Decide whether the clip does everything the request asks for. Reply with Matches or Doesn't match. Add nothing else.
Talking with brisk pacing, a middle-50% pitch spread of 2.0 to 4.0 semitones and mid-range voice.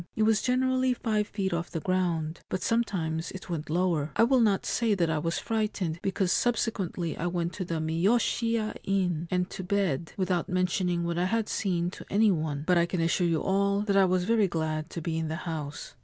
Matches